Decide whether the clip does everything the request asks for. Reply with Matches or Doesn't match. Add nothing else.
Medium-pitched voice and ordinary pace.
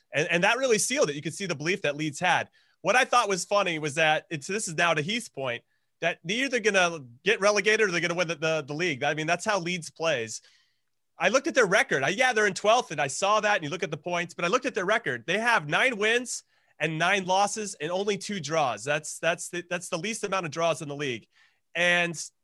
Doesn't match